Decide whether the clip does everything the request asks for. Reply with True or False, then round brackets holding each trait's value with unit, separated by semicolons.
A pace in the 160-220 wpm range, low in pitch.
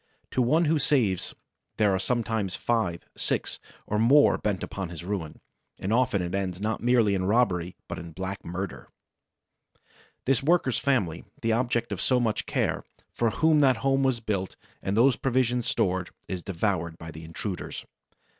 True (165 wpm; 105 Hz)